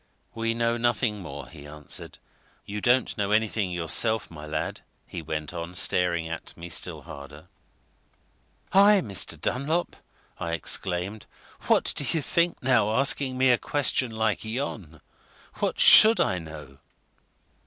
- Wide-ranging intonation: Yes, wide, 6.8 semitones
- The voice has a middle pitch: No, low, 105 Hz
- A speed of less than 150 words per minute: Yes, average, 140 wpm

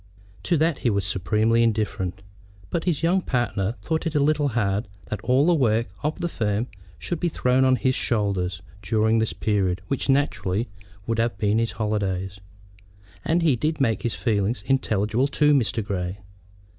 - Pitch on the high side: No, low, 115 Hz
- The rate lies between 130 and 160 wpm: No, average, 175 wpm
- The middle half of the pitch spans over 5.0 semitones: Yes, wide, 5.4 semitones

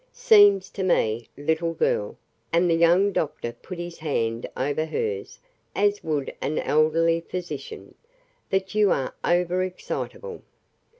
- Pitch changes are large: No, average, 3.8 semitones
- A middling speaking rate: No, slow, 130 wpm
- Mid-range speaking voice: Yes, medium, 170 Hz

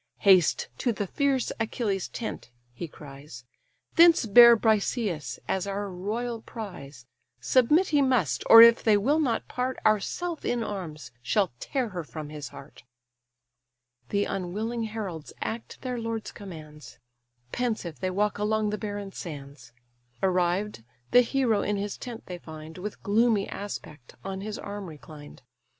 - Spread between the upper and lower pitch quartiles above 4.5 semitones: Yes, average, 5.1 semitones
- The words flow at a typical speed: Yes, average, 145 wpm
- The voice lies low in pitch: No, high, 205 Hz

